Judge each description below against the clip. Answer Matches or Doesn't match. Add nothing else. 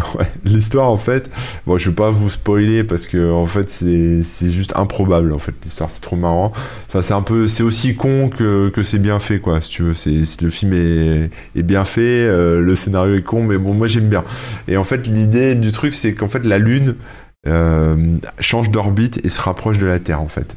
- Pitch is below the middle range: Matches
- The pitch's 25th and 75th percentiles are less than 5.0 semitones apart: Matches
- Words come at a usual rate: Doesn't match